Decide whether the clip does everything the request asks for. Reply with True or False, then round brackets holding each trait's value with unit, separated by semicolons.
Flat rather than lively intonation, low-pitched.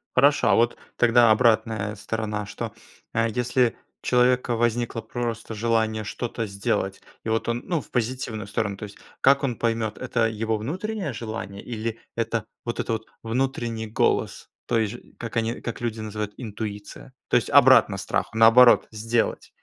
True (1.7 semitones; 115 Hz)